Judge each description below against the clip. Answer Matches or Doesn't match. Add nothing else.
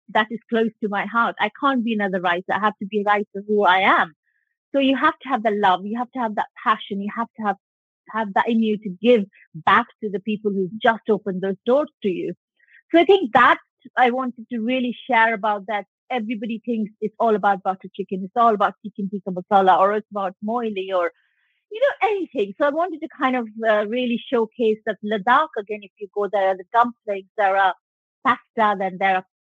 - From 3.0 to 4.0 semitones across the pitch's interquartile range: Matches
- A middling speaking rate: Doesn't match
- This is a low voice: Doesn't match